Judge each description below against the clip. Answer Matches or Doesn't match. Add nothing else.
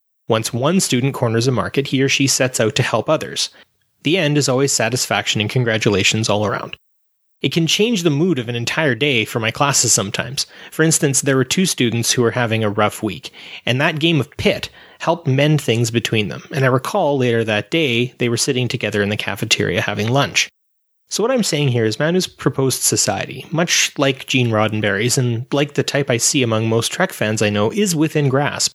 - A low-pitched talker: Matches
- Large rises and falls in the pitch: Doesn't match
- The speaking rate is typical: Doesn't match